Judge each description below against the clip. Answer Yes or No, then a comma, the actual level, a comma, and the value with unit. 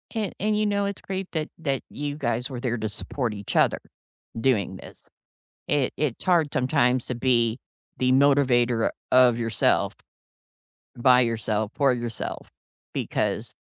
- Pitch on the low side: Yes, low, 130 Hz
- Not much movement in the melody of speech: No, average, 3.8 semitones